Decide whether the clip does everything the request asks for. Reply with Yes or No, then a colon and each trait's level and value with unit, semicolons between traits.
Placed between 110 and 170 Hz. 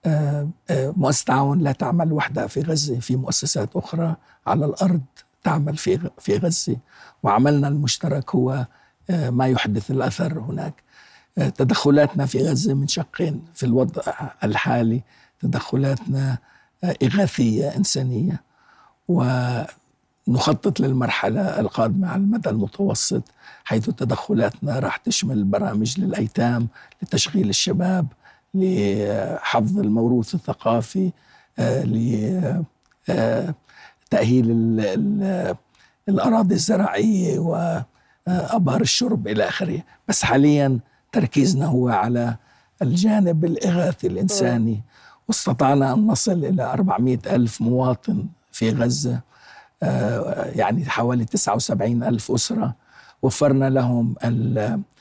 Yes: medium, 140 Hz